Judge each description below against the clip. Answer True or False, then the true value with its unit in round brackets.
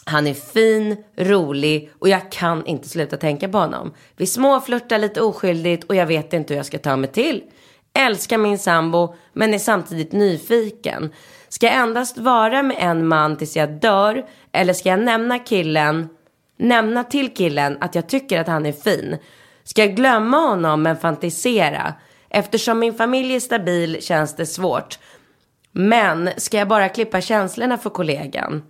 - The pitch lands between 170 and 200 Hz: True (190 Hz)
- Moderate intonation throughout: False (5.7 semitones)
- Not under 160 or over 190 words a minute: True (165 wpm)